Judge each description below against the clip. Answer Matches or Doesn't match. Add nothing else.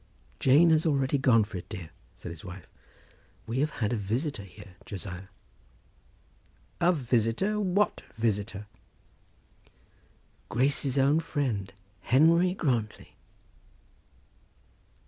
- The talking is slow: Matches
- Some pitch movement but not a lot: Doesn't match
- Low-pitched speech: Matches